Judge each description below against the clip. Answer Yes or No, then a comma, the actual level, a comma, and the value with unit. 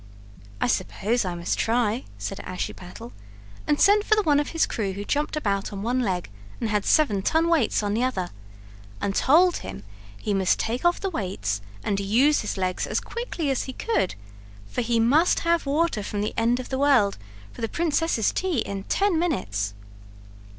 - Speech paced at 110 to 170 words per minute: No, average, 190 wpm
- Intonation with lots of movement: Yes, wide, 7.7 semitones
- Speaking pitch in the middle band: No, high, 230 Hz